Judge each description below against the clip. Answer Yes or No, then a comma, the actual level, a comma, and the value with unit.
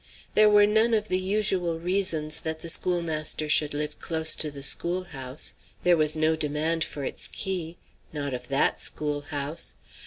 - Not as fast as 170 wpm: Yes, average, 160 wpm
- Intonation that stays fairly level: No, average, 3.4 semitones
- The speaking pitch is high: No, medium, 160 Hz